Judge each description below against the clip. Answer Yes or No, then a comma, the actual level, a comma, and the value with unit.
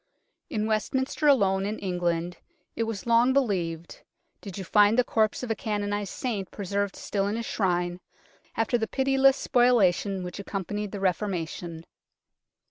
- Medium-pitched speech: No, high, 205 Hz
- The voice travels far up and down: No, average, 3.5 semitones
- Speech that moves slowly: No, average, 145 wpm